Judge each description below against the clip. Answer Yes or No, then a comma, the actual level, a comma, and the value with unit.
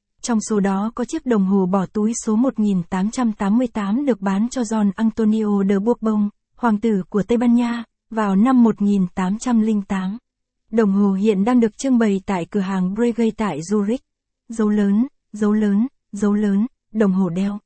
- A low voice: No, high, 215 Hz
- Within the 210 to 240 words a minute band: No, slow, 165 wpm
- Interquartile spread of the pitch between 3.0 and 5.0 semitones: No, narrow, 2.5 semitones